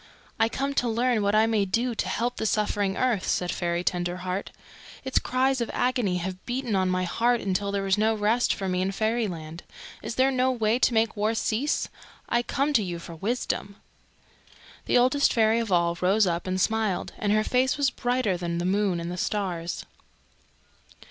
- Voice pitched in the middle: No, high, 215 Hz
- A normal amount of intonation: Yes, average, 4.7 semitones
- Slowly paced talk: No, average, 190 wpm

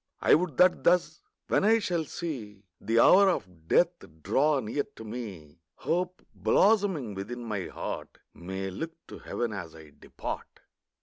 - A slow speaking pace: No, average, 150 wpm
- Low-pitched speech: Yes, low, 120 Hz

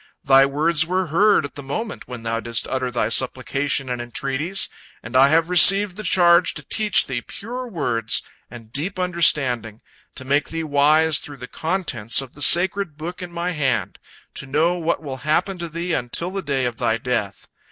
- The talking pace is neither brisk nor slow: Yes, average, 190 wpm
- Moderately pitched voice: Yes, medium, 150 Hz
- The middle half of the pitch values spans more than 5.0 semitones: Yes, wide, 5.4 semitones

